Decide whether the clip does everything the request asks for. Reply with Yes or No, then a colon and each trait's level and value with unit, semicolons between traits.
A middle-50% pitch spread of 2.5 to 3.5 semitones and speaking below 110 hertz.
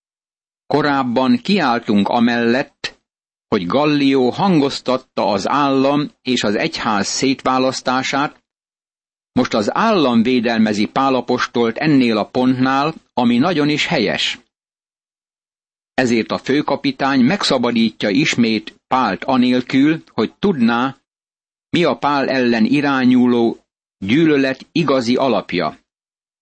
No: average, 3.0 semitones; low, 130 Hz